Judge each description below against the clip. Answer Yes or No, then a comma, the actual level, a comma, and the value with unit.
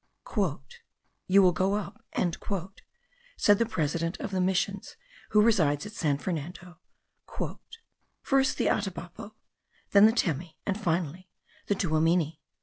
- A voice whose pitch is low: No, medium, 185 Hz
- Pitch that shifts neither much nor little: Yes, average, 3.7 semitones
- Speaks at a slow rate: Yes, slow, 120 wpm